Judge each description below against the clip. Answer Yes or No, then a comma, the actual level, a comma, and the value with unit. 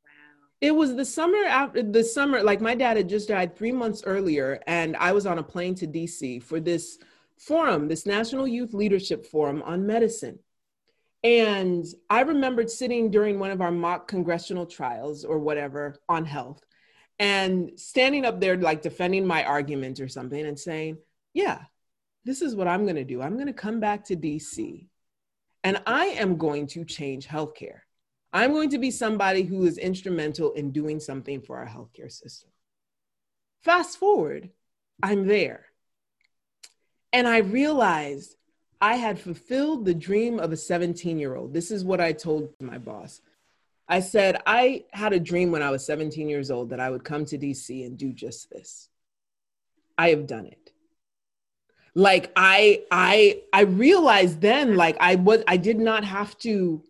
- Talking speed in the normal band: Yes, average, 170 wpm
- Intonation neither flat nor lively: No, wide, 6.5 semitones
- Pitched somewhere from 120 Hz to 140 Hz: No, medium, 185 Hz